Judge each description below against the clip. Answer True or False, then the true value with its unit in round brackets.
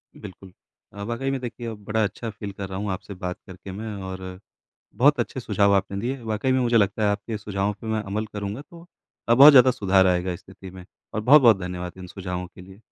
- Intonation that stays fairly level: False (3.6 semitones)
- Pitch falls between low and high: False (105 Hz)